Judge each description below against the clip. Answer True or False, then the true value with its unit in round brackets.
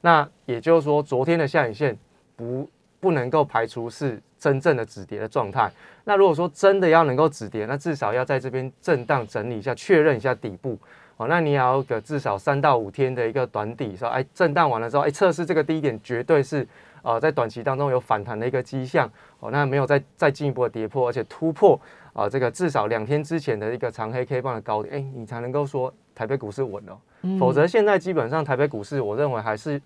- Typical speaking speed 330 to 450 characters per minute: True (340 characters per minute)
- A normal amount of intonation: True (4.6 semitones)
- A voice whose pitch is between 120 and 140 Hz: True (135 Hz)